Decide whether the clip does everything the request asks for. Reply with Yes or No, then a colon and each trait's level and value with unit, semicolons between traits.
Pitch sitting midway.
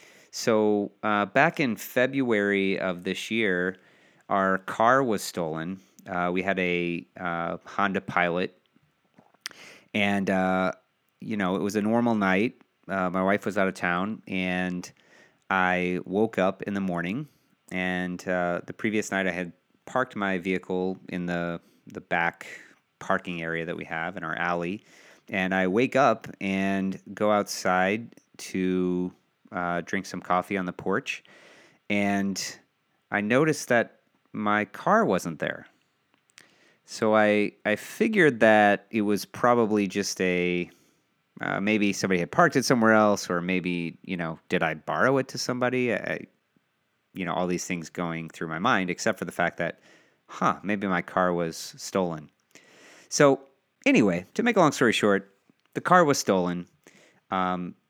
No: very low, 95 Hz